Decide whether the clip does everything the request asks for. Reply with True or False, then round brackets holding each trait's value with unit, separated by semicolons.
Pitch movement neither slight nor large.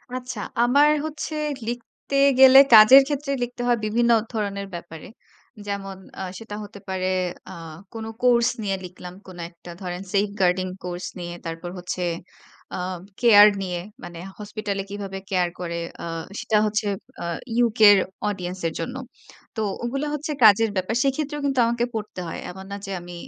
True (4.6 semitones)